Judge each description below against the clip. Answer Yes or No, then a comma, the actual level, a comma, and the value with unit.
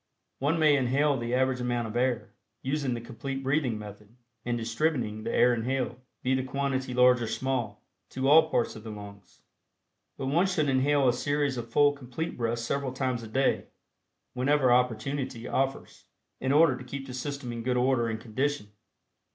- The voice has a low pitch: Yes, low, 130 Hz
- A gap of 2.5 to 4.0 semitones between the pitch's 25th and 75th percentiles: Yes, average, 2.8 semitones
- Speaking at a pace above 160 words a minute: Yes, average, 180 wpm